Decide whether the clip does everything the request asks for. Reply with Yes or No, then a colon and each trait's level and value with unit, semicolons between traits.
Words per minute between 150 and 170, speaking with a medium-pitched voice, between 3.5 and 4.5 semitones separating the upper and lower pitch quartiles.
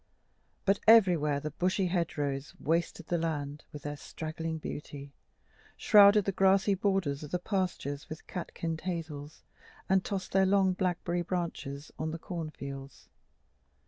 No: average, 140 wpm; medium, 165 Hz; average, 4.2 semitones